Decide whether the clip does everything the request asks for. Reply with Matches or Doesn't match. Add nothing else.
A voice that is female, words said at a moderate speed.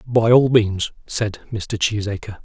Doesn't match